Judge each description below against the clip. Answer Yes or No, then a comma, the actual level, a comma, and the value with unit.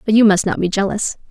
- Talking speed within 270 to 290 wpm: Yes, fast, 275 wpm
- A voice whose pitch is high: Yes, high, 205 Hz